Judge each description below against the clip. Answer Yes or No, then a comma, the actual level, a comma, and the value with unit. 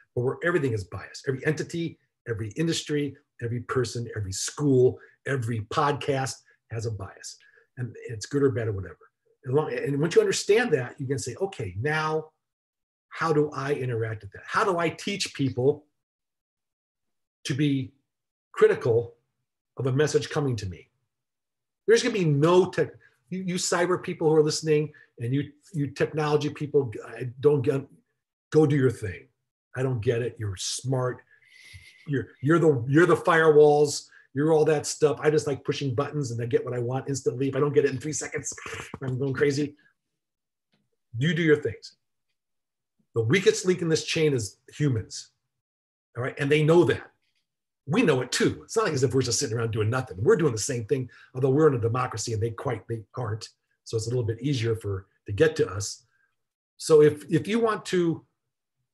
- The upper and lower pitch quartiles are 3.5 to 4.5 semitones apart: Yes, average, 4.2 semitones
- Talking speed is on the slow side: No, average, 190 wpm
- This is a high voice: No, medium, 140 Hz